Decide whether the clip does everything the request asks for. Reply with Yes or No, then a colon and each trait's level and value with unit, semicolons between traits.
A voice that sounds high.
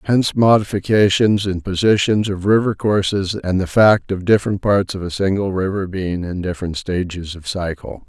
No: very low, 95 Hz